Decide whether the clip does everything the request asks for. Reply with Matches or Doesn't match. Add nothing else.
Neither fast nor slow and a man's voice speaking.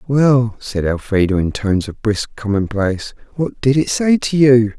Matches